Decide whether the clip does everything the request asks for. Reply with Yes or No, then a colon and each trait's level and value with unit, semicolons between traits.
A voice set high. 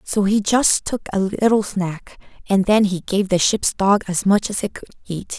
Yes: high, 200 Hz